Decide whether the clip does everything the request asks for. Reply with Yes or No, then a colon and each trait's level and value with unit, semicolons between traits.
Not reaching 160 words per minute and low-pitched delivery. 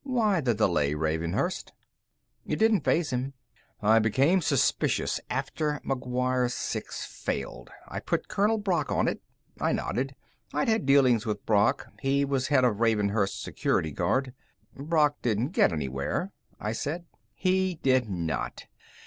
Yes: average, 140 wpm; low, 130 Hz